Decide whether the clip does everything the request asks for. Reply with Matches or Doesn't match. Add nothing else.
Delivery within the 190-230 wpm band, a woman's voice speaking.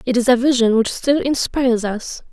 Matches